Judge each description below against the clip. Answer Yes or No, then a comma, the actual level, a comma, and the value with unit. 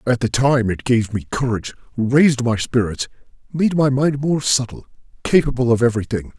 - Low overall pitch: Yes, low, 125 Hz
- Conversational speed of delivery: Yes, average, 170 wpm